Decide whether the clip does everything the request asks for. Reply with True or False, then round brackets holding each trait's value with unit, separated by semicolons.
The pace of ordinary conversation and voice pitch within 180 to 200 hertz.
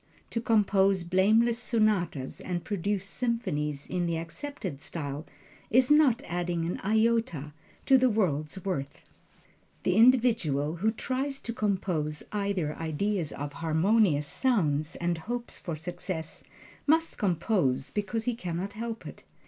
False (130 wpm; 190 Hz)